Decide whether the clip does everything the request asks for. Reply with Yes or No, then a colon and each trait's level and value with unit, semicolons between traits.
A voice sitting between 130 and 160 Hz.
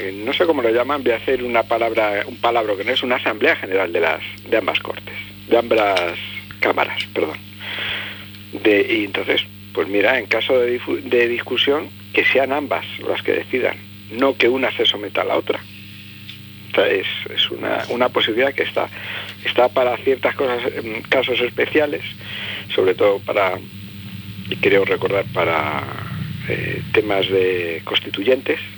No: low, 100 Hz